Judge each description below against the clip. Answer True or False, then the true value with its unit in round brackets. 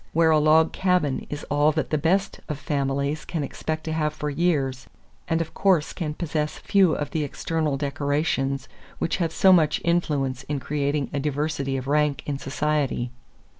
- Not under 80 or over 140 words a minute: False (175 wpm)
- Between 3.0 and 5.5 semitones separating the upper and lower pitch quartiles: False (2.4 semitones)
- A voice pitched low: False (150 Hz)